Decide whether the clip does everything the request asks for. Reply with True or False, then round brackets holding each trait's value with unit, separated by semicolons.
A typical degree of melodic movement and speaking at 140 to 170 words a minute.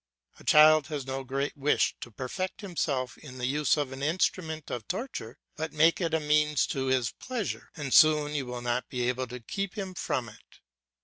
False (3.6 semitones; 200 wpm)